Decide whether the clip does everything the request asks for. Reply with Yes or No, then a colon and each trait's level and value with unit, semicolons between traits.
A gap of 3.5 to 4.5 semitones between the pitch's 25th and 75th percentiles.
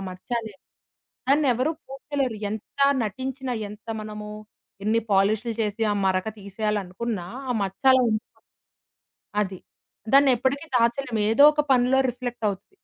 Yes: average, 4.0 semitones